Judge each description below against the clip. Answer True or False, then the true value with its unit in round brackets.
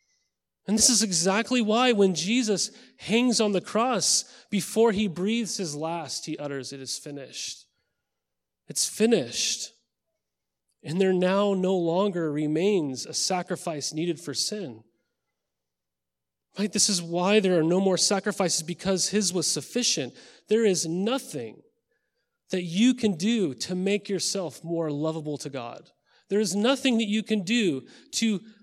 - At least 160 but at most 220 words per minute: False (145 wpm)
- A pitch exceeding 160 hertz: True (190 Hz)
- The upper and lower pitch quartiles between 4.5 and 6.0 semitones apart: True (5.2 semitones)